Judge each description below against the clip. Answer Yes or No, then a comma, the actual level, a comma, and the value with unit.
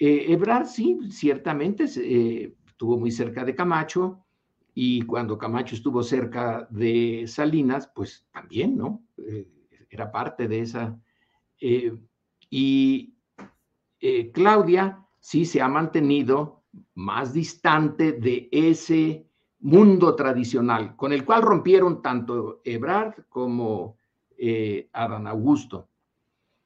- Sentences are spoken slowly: Yes, slow, 110 wpm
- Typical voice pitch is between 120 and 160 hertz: Yes, medium, 140 Hz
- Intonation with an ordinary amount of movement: No, wide, 7.3 semitones